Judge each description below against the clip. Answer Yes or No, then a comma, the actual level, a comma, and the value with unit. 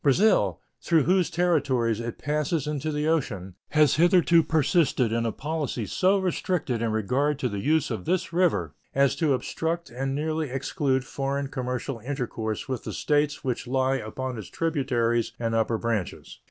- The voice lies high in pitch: No, low, 135 Hz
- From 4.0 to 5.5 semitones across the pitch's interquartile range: Yes, average, 5.1 semitones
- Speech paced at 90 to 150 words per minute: No, average, 165 wpm